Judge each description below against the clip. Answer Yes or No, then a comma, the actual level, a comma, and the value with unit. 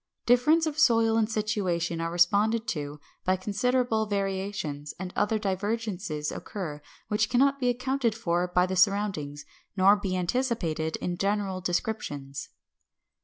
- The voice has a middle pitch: No, high, 200 Hz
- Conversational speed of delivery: No, slow, 130 wpm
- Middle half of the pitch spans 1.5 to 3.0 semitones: No, average, 4.4 semitones